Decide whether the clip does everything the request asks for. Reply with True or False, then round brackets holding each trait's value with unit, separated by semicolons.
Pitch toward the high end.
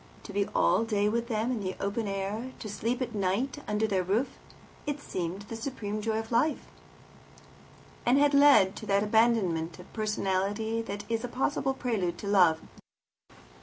True (215 Hz)